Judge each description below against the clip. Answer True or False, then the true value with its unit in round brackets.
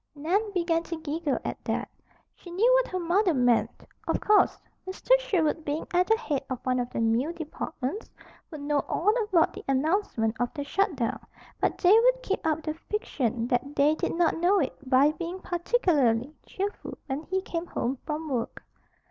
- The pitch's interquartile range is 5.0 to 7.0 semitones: True (5.5 semitones)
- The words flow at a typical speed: True (185 wpm)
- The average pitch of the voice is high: True (320 Hz)